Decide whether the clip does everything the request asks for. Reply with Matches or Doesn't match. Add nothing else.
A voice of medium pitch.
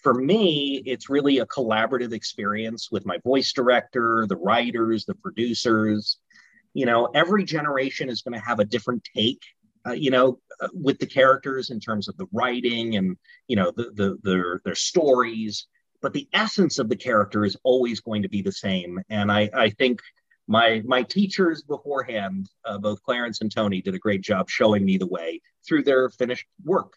Doesn't match